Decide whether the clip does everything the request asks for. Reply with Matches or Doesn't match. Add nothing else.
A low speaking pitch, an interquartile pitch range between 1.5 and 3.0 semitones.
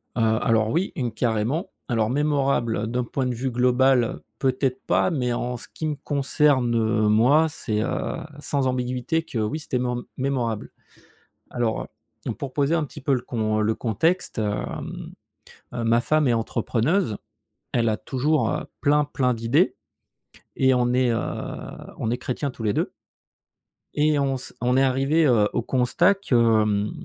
Doesn't match